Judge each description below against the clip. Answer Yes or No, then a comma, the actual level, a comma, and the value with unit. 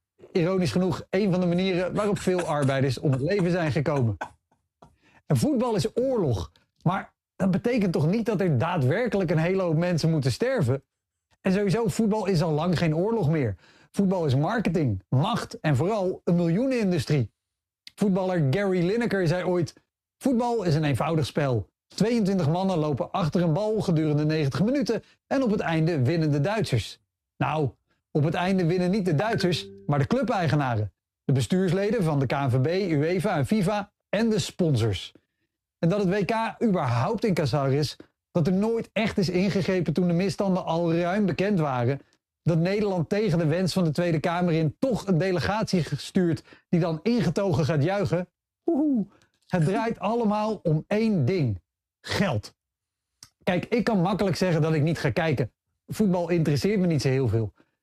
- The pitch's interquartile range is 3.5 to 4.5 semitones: No, average, 4.9 semitones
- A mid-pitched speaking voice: Yes, medium, 175 Hz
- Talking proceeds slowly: No, average, 170 wpm